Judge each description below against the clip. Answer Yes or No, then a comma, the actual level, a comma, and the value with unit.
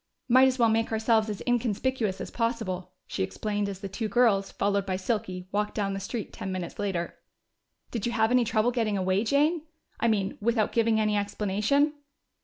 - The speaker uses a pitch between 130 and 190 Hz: No, high, 215 Hz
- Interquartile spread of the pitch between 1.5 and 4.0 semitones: Yes, average, 3.0 semitones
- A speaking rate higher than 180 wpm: Yes, average, 190 wpm